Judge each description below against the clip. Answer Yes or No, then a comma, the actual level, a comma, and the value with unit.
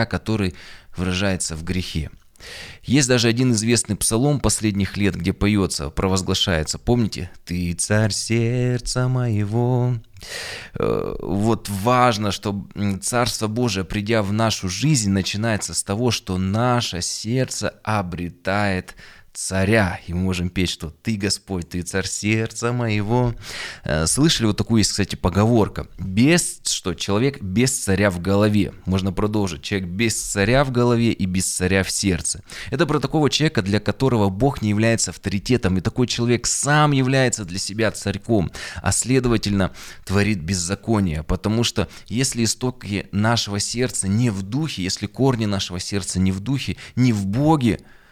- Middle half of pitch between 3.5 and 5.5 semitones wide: Yes, average, 3.9 semitones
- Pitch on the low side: Yes, low, 105 Hz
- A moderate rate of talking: Yes, average, 140 wpm